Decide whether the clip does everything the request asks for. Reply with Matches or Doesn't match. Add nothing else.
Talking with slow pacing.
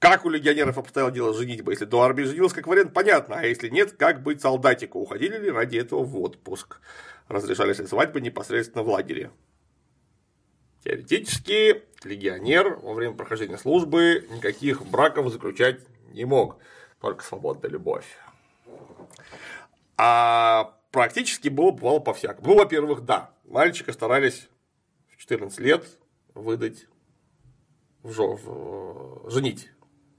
Doesn't match